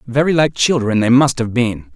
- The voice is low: Yes, low, 125 Hz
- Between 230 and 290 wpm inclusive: No, fast, 215 wpm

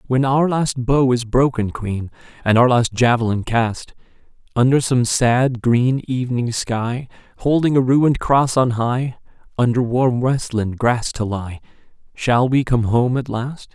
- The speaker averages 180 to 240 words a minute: No, average, 155 wpm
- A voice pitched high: No, low, 125 Hz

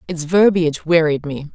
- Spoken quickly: No, average, 155 wpm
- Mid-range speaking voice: Yes, medium, 165 Hz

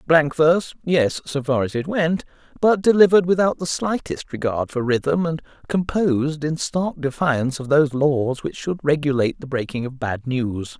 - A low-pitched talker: No, medium, 150 Hz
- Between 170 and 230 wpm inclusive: Yes, average, 180 wpm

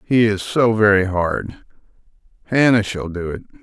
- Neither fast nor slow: Yes, average, 150 wpm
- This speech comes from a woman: No, male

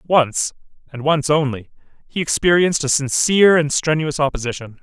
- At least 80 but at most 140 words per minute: Yes, slow, 135 wpm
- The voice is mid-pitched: Yes, medium, 150 Hz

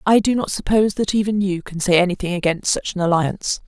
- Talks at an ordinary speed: No, fast, 230 wpm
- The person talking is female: Yes, female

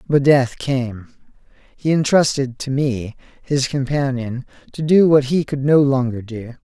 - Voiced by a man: Yes, male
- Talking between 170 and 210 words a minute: No, average, 145 wpm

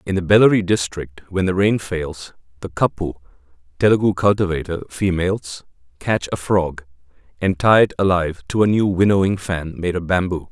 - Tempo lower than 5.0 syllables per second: No, 5.3 syllables/s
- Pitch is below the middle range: Yes, very low, 90 Hz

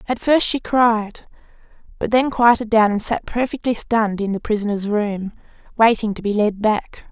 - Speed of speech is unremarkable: Yes, average, 175 wpm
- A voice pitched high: Yes, high, 220 Hz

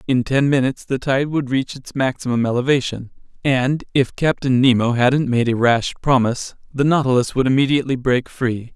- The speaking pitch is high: No, low, 130 Hz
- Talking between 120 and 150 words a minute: No, average, 170 wpm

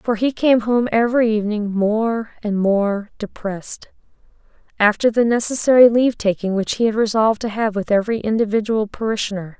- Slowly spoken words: No, average, 155 wpm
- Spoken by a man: No, female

